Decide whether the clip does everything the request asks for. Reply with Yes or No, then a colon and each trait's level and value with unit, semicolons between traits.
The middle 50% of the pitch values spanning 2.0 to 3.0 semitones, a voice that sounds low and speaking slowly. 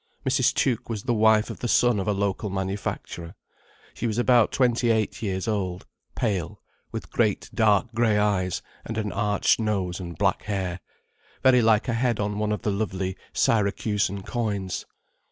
No: average, 2.7 semitones; low, 105 Hz; average, 170 wpm